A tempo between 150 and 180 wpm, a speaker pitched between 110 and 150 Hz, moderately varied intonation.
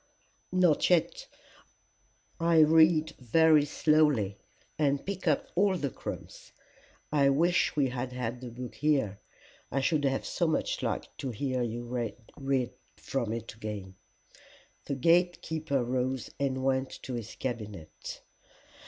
No: slow, 135 wpm; low, 135 Hz; average, 4.4 semitones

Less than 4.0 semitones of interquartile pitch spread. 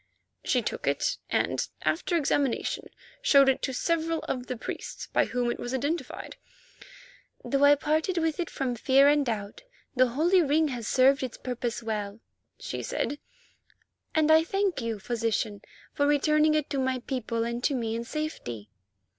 No: average, 4.4 semitones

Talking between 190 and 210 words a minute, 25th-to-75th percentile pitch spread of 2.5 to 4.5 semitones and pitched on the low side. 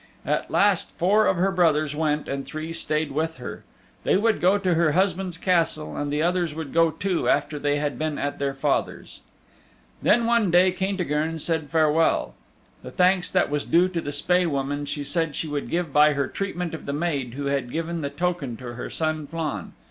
No: average, 200 wpm; average, 3.5 semitones; medium, 160 Hz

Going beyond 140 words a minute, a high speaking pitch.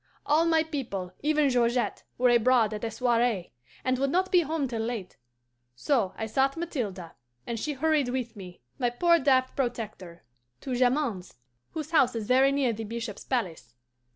Yes: average, 170 wpm; high, 245 Hz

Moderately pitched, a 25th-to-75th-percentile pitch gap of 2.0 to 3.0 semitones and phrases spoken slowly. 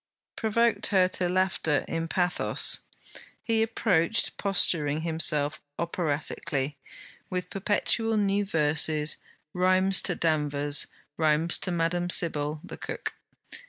No: medium, 170 Hz; average, 3.9 semitones; slow, 105 wpm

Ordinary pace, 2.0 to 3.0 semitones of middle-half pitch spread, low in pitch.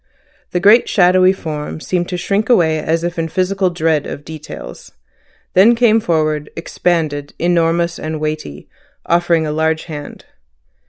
No: average, 145 wpm; narrow, 2.6 semitones; medium, 165 Hz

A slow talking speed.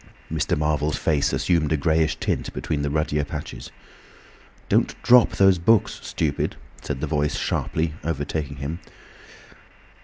Yes: slow, 125 wpm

